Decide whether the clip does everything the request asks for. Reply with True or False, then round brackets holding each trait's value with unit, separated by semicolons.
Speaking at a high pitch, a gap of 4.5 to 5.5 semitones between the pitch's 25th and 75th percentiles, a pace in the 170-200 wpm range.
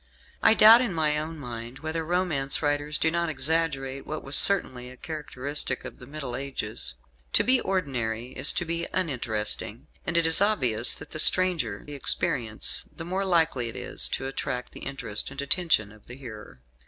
False (140 Hz; 4.9 semitones; 180 wpm)